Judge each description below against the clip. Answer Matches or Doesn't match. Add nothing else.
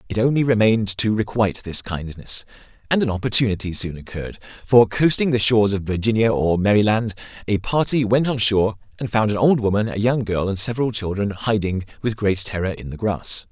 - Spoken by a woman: Doesn't match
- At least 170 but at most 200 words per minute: Matches